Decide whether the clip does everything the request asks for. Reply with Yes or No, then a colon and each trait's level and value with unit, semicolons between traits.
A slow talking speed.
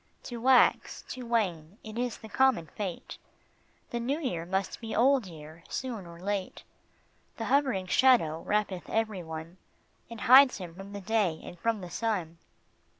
No: average, 160 wpm